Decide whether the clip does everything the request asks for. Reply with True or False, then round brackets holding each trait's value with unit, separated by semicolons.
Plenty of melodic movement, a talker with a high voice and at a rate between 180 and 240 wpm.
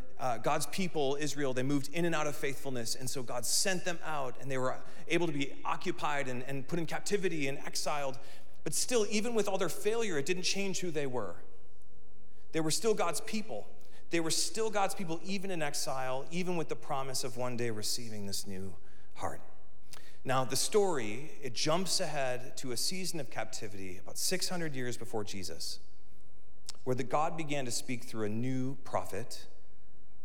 False (6.1 semitones; 145 Hz; 185 wpm)